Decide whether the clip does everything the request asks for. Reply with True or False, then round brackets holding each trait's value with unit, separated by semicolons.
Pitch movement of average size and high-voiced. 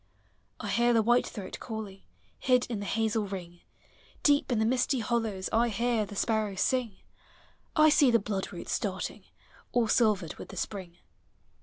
True (3.2 semitones; 220 Hz)